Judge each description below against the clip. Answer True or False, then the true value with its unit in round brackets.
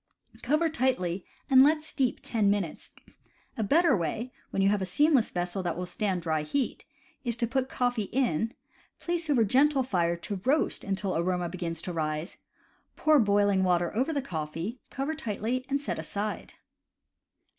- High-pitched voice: True (210 Hz)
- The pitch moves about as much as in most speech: False (6.9 semitones)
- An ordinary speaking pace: True (165 wpm)